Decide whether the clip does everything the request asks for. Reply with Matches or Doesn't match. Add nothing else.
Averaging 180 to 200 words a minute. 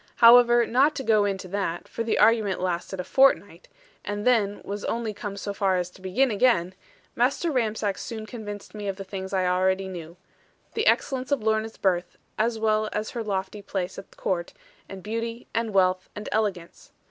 Matches